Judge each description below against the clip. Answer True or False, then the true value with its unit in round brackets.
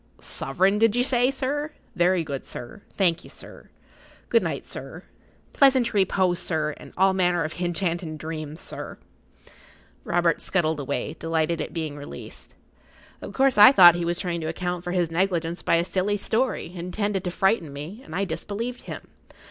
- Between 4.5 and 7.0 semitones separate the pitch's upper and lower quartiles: False (3.7 semitones)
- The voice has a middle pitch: True (175 Hz)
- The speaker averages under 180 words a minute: True (170 wpm)